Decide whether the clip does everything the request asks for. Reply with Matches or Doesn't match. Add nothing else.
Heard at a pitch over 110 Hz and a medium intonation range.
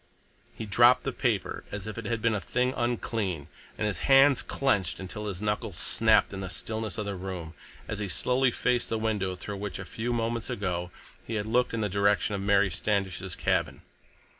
Doesn't match